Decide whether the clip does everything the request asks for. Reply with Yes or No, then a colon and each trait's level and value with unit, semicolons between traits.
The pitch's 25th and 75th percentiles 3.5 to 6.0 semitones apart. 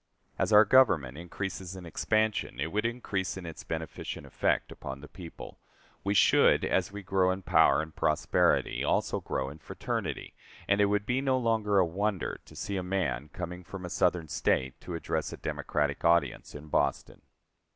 Yes: average, 4.1 semitones